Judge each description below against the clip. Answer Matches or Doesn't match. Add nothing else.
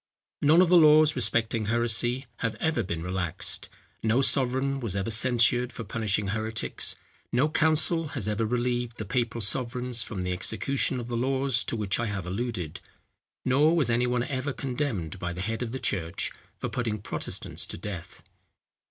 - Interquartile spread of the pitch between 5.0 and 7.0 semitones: Doesn't match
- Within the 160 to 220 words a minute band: Matches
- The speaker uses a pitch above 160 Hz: Doesn't match